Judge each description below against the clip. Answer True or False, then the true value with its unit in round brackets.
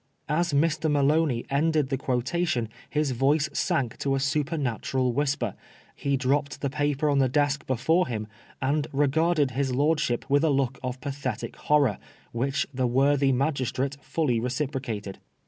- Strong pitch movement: False (2.6 semitones)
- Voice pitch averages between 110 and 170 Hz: True (140 Hz)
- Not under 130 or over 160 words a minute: True (145 wpm)